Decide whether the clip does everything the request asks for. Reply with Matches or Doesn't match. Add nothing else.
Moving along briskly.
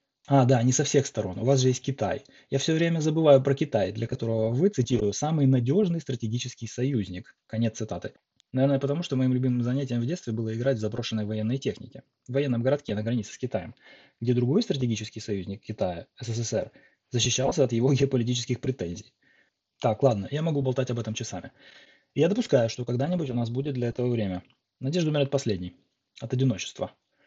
Matches